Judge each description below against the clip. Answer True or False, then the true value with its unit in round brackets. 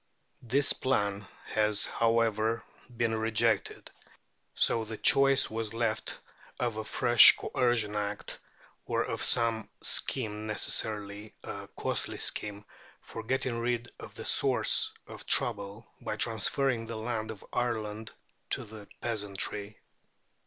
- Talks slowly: True (120 wpm)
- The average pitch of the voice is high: False (110 Hz)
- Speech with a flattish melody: True (1.8 semitones)